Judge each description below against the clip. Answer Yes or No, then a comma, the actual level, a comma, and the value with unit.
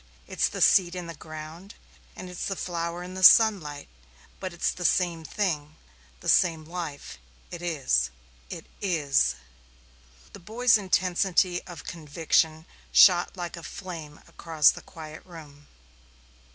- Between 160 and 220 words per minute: No, average, 140 wpm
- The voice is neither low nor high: Yes, medium, 170 Hz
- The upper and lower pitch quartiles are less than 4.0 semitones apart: Yes, average, 2.8 semitones